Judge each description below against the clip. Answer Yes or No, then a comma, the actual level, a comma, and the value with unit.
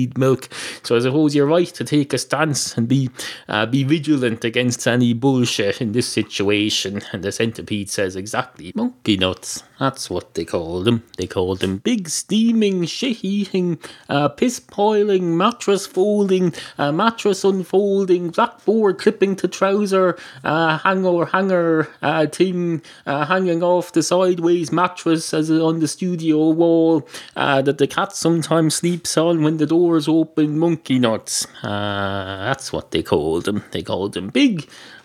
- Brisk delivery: No, average, 150 wpm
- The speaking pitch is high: No, medium, 160 Hz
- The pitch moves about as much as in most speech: No, wide, 6.1 semitones